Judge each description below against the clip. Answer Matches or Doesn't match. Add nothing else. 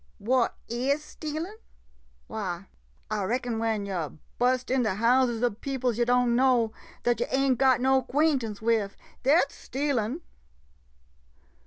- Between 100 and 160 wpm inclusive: Matches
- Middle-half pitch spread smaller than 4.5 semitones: Matches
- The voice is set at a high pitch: Matches